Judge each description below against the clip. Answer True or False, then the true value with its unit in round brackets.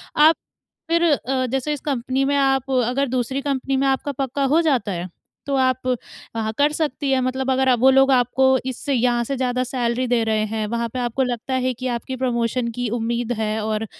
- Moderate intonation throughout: False (2.2 semitones)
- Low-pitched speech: False (255 Hz)